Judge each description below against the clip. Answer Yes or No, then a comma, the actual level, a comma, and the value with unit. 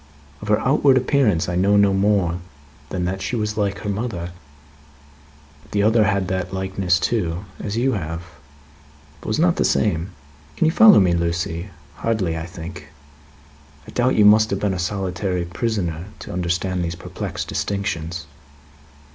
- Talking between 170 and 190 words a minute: No, average, 160 wpm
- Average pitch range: Yes, average, 3.5 semitones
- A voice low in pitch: Yes, very low, 95 Hz